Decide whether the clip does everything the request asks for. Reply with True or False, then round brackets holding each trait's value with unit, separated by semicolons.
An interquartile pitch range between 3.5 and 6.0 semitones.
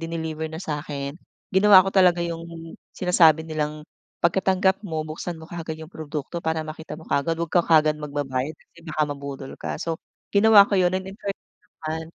False (2.8 semitones)